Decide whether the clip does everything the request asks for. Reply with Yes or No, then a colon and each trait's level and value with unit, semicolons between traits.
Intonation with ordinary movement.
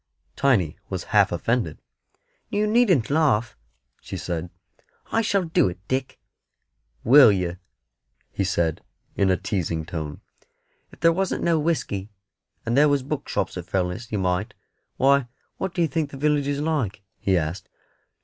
No: wide, 8.6 semitones